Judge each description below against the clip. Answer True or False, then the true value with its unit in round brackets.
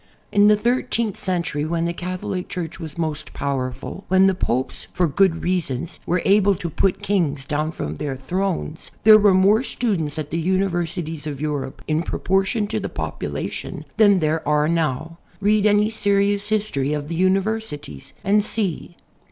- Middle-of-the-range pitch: True (180 Hz)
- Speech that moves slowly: False (165 wpm)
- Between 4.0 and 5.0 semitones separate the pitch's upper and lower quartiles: True (4.7 semitones)